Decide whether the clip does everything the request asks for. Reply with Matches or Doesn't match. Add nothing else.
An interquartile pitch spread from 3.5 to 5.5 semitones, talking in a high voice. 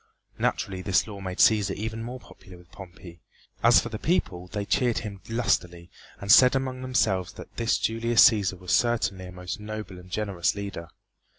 Doesn't match